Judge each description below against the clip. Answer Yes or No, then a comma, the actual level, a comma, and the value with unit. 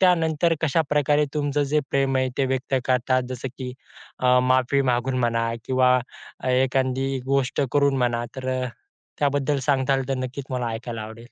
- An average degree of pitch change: No, narrow, 1.9 semitones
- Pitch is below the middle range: Yes, low, 130 Hz